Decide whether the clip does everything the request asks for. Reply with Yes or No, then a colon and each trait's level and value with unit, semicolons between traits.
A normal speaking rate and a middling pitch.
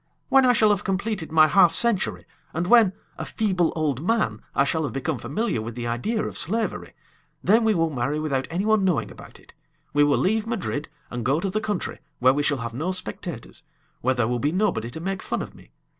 No: fast, 220 wpm; medium, 165 Hz